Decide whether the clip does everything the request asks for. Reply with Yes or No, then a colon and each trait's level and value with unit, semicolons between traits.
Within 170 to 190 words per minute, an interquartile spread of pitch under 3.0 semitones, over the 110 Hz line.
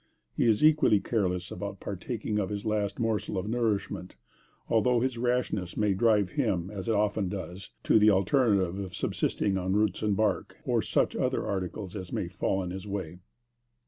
No: average, 175 wpm; narrow, 2.6 semitones; low, 100 Hz